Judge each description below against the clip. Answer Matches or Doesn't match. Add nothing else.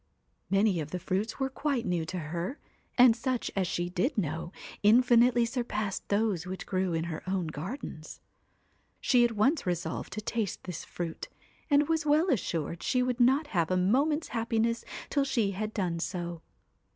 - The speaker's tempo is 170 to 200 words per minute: Matches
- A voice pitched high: Matches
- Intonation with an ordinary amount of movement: Doesn't match